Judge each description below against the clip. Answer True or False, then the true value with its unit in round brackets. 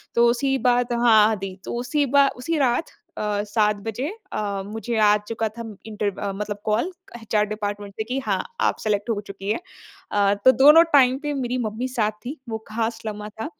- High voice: True (220 Hz)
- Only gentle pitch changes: False (3.0 semitones)